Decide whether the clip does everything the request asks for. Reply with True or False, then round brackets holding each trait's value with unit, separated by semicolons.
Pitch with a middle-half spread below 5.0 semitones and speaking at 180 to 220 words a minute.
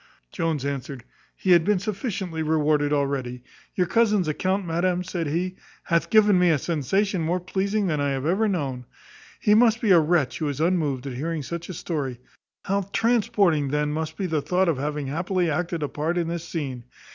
True (4.2 semitones; 190 wpm)